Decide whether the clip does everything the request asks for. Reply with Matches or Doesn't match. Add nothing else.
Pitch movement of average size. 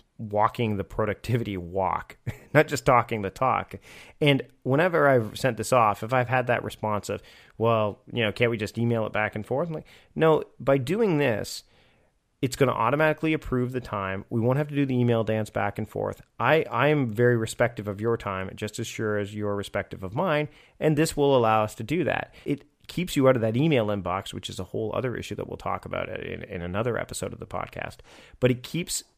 Matches